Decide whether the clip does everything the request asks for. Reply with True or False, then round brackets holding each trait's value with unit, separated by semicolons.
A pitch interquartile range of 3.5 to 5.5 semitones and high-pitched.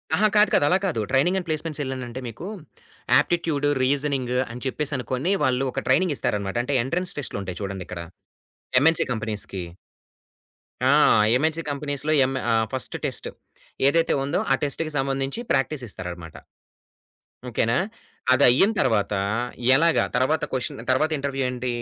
False (4.0 semitones; 135 Hz)